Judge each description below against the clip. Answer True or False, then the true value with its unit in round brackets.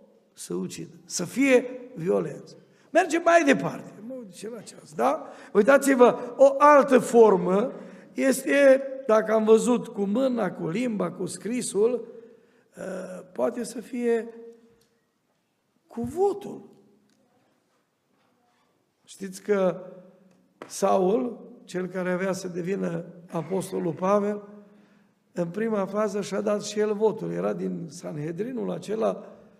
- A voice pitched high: True (210 Hz)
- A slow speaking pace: True (105 wpm)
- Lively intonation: False (4.4 semitones)